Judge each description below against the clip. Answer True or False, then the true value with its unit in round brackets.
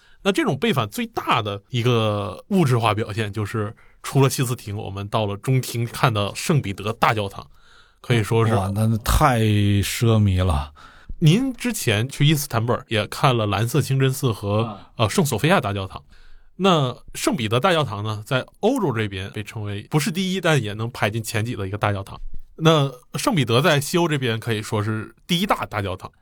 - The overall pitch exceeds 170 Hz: False (115 Hz)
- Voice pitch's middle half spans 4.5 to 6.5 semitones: True (5.1 semitones)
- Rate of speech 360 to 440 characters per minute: False (285 characters per minute)